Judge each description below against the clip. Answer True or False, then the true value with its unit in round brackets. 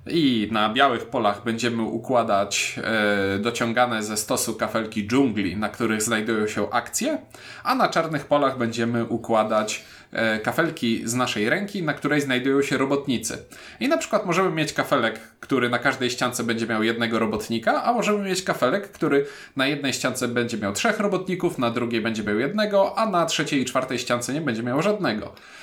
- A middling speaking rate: False (175 wpm)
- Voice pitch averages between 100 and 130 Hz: True (120 Hz)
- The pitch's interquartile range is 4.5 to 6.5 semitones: True (4.9 semitones)